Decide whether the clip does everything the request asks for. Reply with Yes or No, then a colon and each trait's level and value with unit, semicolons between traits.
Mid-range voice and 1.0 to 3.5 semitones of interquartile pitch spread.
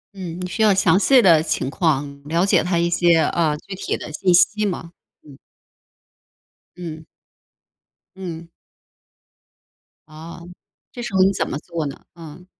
Yes: medium, 170 Hz; average, 2.9 semitones